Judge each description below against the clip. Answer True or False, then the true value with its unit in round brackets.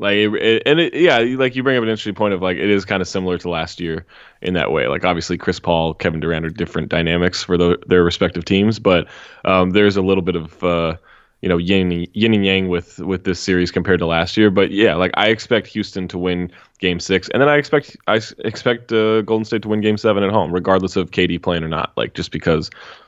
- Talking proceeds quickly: True (250 wpm)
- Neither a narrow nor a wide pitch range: True (3.3 semitones)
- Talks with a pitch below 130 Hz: True (95 Hz)